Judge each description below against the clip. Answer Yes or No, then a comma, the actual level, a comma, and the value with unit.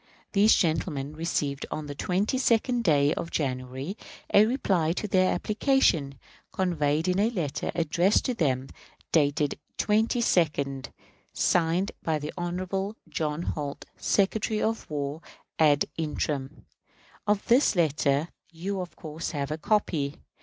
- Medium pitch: Yes, medium, 165 Hz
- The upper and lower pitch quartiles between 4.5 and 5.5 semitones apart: Yes, average, 5.2 semitones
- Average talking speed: No, slow, 130 wpm